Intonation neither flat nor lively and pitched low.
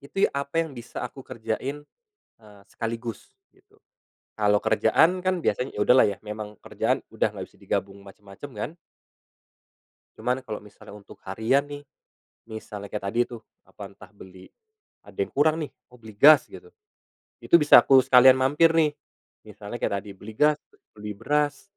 No: wide, 5.9 semitones; low, 120 Hz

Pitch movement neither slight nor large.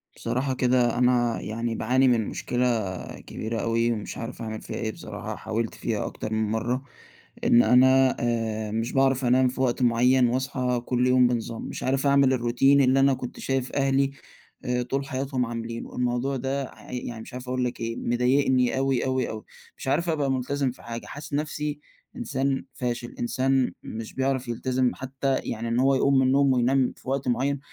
No: narrow, 2.0 semitones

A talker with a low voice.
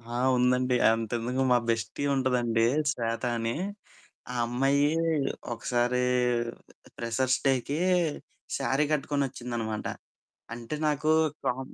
Yes: low, 125 Hz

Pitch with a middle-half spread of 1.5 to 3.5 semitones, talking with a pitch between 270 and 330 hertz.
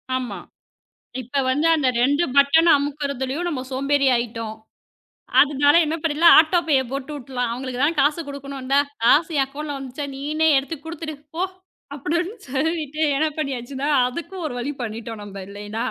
Yes: average, 3.2 semitones; very high, 280 Hz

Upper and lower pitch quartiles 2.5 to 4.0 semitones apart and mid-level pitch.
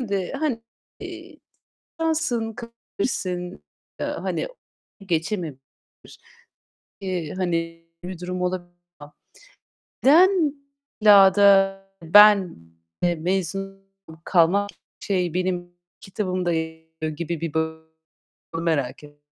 Yes: average, 3.3 semitones; medium, 180 Hz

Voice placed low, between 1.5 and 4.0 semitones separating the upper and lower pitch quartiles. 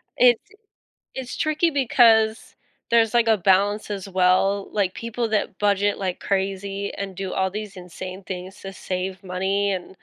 No: high, 200 Hz; narrow, 2.6 semitones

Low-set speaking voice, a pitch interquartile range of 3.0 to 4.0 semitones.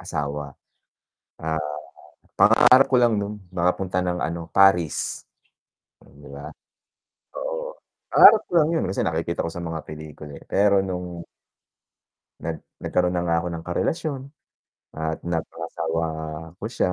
Yes: very low, 85 Hz; average, 3.7 semitones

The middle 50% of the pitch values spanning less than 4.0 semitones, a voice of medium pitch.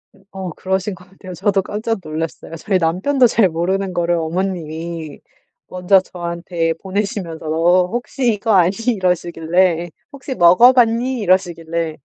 Yes: average, 3.2 semitones; medium, 180 Hz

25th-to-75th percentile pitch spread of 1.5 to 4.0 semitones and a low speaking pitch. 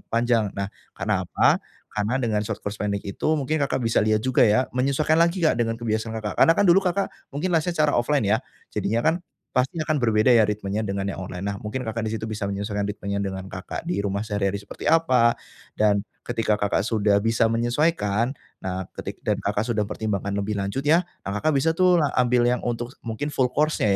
No: average, 4.6 semitones; low, 115 Hz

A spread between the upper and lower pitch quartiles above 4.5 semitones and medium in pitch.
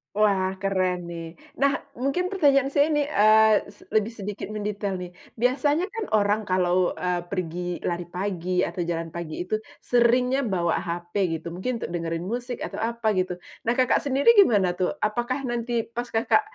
No: wide, 5.5 semitones; high, 205 Hz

